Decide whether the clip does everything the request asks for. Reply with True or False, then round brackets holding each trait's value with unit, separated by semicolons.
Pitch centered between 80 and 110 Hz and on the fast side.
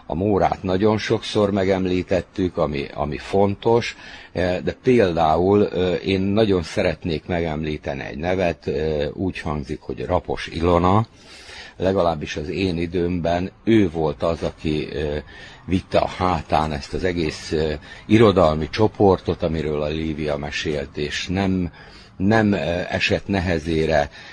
False (90 Hz; 115 wpm)